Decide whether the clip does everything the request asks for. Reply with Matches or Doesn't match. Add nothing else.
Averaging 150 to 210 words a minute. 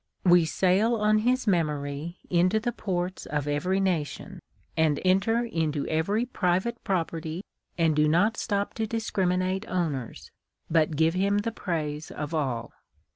Doesn't match